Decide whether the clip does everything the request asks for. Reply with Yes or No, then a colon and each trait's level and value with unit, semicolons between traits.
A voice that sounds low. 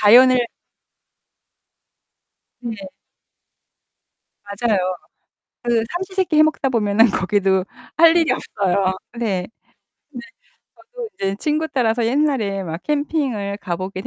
No: high, 230 Hz